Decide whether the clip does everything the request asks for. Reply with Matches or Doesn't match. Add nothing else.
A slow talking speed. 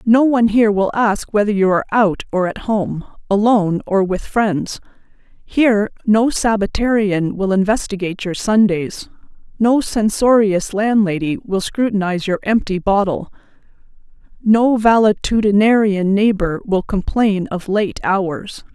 Matches